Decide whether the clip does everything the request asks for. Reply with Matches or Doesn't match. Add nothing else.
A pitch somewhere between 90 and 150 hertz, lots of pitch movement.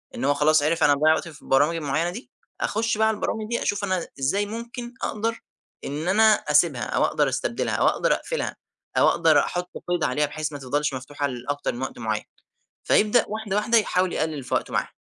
Doesn't match